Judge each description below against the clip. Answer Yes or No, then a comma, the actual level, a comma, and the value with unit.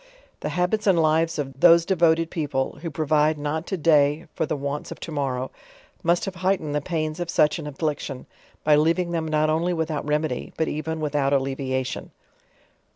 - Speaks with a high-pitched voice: No, medium, 155 Hz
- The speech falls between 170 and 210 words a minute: Yes, average, 195 wpm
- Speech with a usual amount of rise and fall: No, narrow, 2.3 semitones